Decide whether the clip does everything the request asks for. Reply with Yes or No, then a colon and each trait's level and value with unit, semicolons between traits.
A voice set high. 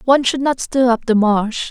Yes: high, 245 Hz